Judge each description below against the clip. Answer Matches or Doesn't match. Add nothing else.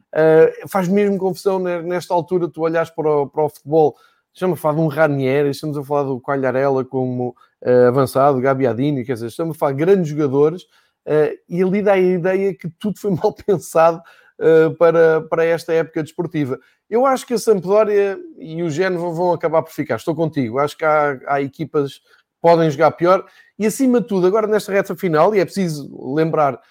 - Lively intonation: Doesn't match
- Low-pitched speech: Doesn't match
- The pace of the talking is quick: Matches